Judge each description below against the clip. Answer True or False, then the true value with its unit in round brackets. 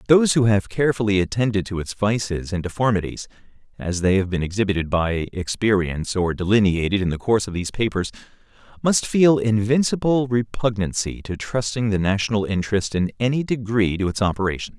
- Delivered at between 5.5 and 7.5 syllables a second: True (5.9 syllables/s)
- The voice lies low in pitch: True (105 Hz)